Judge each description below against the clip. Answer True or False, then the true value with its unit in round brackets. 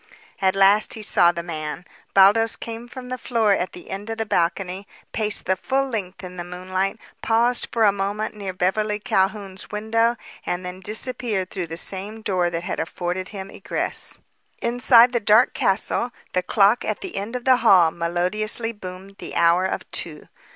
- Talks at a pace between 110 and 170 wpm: False (180 wpm)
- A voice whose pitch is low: False (195 Hz)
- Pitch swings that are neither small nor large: True (3.5 semitones)